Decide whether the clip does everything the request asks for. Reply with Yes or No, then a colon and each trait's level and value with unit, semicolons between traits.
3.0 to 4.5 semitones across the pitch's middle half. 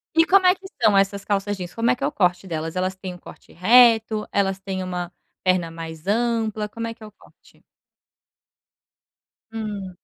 Yes: average, 3.8 semitones